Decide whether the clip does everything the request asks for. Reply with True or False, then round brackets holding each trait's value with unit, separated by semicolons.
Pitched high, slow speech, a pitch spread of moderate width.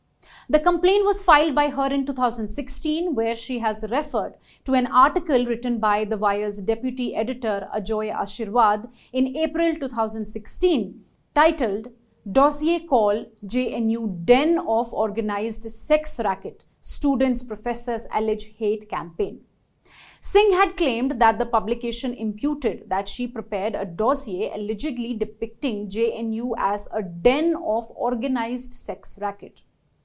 True (235 Hz; 125 wpm; 4.0 semitones)